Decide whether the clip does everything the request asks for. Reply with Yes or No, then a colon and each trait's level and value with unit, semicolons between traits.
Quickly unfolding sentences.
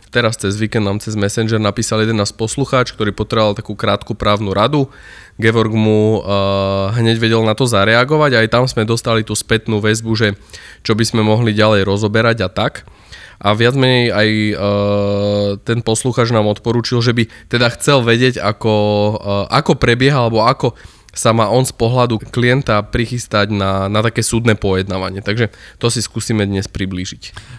Yes: fast, 170 wpm